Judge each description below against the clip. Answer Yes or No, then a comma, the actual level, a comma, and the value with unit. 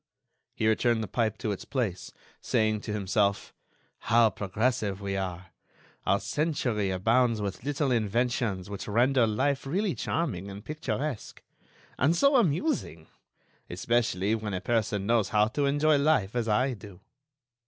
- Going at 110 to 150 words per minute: Yes, average, 145 wpm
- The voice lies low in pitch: Yes, low, 110 Hz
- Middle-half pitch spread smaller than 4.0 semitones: No, average, 5.0 semitones